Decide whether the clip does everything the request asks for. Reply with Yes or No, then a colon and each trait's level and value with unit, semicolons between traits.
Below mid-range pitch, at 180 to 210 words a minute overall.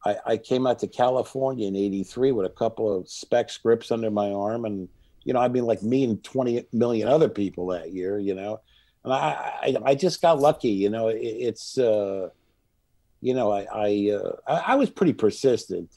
Yes: low, 110 Hz; fast, 205 wpm